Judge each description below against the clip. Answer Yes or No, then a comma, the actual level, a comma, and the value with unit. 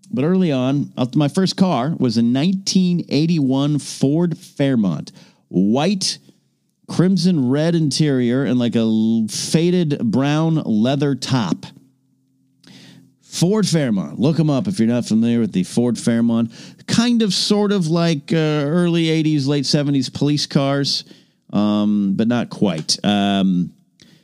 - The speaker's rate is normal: No, slow, 130 wpm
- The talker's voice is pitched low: No, medium, 145 Hz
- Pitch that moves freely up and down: Yes, wide, 5.7 semitones